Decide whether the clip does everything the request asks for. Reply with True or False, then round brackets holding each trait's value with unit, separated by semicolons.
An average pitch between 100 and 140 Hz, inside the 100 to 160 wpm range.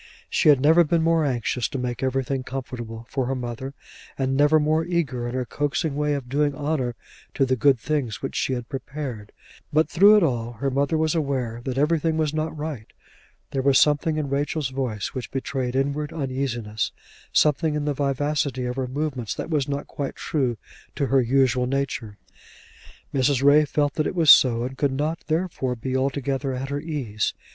False (135 Hz; 190 wpm)